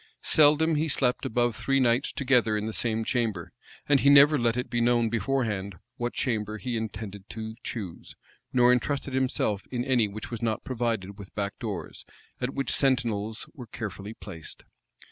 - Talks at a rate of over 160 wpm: Yes, average, 170 wpm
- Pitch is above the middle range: No, low, 120 Hz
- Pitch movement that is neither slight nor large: Yes, average, 3.3 semitones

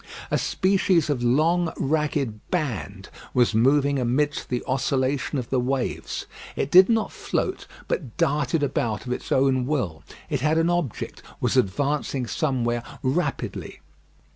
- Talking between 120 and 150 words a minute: Yes, average, 140 wpm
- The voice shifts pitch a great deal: No, average, 3.7 semitones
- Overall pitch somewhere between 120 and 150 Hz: Yes, low, 135 Hz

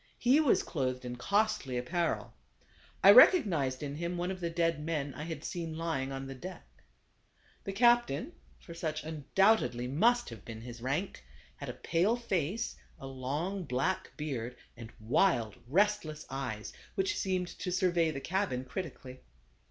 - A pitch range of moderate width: No, wide, 6.3 semitones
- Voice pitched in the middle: Yes, medium, 160 Hz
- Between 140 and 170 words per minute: Yes, average, 155 wpm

